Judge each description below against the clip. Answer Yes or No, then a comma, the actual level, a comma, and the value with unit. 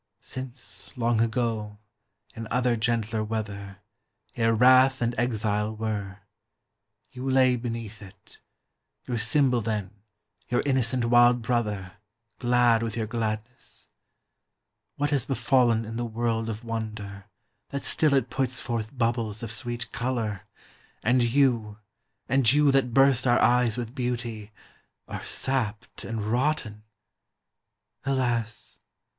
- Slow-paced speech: Yes, slow, 120 wpm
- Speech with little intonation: Yes, narrow, 2.3 semitones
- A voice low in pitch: Yes, low, 115 Hz